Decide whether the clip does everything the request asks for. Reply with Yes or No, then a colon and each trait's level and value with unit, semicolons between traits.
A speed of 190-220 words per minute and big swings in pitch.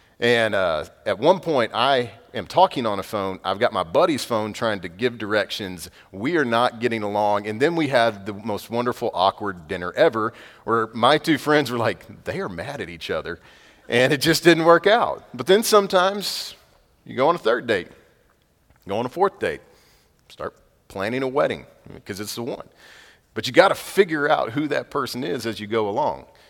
Yes: average, 200 wpm; wide, 6.1 semitones